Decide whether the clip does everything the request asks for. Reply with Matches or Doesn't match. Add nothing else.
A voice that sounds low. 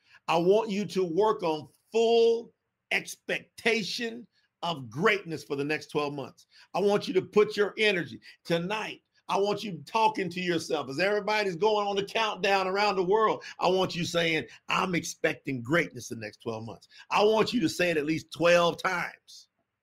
Doesn't match